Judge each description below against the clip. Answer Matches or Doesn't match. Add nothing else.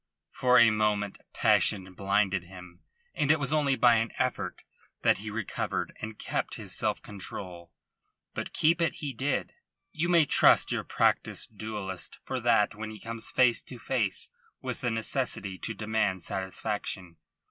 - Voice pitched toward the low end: Matches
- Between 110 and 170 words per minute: Matches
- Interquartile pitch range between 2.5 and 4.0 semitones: Doesn't match